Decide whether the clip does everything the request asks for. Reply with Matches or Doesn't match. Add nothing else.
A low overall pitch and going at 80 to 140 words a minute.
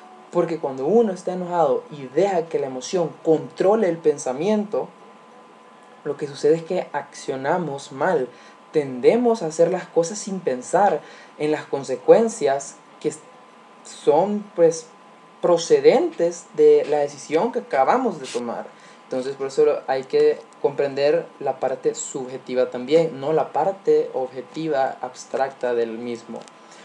Doesn't match